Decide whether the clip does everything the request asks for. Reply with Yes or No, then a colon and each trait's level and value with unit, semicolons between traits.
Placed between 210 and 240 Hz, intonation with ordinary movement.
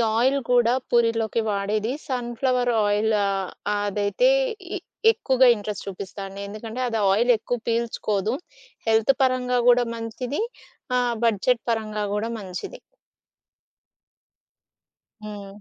Yes: high, 225 Hz; average, 3.0 semitones